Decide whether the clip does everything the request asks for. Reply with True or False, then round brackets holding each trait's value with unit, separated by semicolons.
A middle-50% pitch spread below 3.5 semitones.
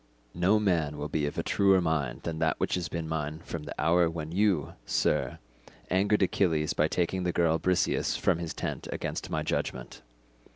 True (2.8 semitones)